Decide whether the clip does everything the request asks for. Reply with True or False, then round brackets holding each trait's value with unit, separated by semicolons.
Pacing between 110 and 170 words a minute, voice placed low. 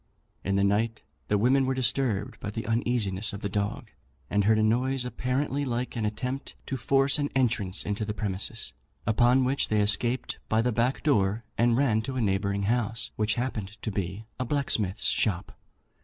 False (185 wpm; 115 Hz)